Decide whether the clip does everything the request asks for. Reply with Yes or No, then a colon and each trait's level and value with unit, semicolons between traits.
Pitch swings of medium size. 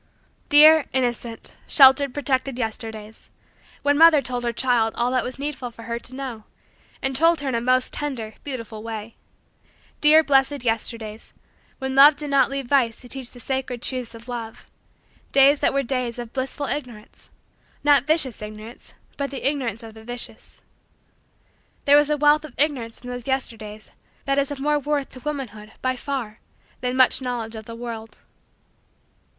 Yes: average, 3.4 semitones